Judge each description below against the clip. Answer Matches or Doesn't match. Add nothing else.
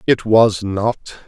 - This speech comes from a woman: Doesn't match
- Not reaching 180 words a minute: Matches